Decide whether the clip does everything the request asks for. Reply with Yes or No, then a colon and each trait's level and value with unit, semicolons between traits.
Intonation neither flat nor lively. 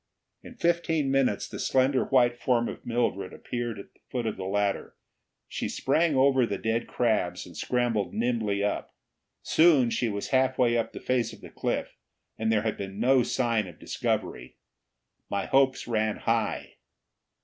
Yes: average, 3.5 semitones